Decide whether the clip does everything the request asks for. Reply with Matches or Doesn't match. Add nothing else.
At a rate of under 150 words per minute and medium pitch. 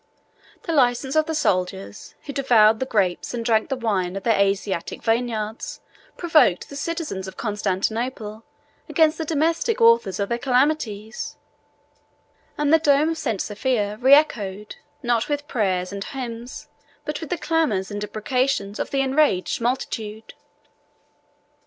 Doesn't match